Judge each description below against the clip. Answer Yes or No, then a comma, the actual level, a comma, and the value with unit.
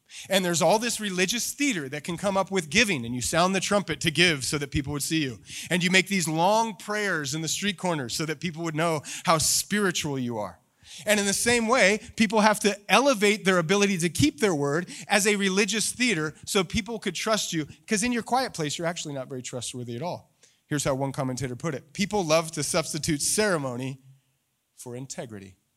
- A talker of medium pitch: Yes, medium, 175 Hz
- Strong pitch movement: Yes, wide, 5.8 semitones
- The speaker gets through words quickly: Yes, fast, 215 wpm